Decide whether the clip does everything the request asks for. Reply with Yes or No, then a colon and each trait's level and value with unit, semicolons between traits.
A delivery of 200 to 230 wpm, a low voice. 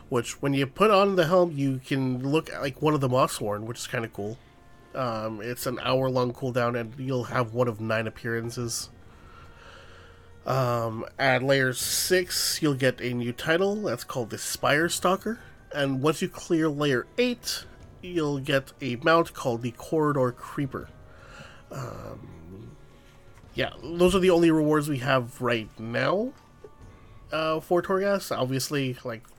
No: average, 155 wpm; low, 130 Hz